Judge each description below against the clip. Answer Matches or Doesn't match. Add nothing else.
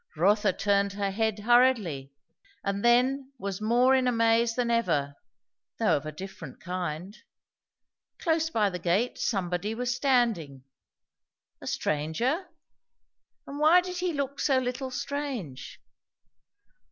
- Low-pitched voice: Doesn't match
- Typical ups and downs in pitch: Doesn't match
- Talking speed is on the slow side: Matches